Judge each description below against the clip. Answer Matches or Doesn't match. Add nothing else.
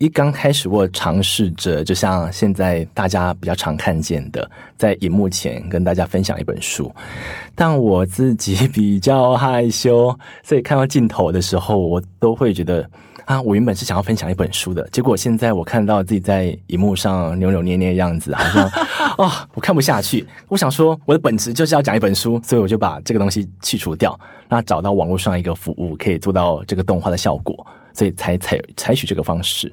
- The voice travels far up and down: Doesn't match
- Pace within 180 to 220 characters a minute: Doesn't match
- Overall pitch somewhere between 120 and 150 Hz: Doesn't match